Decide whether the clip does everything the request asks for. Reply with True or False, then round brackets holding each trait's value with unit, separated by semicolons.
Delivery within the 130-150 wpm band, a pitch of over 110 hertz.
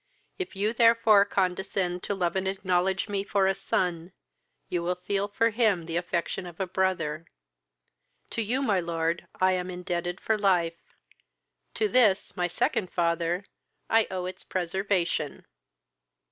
True (145 wpm; 185 Hz)